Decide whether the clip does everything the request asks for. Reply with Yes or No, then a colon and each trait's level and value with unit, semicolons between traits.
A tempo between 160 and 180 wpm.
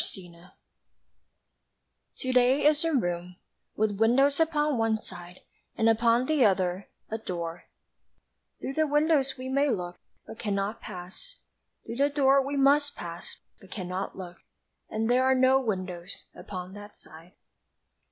No: average, 145 wpm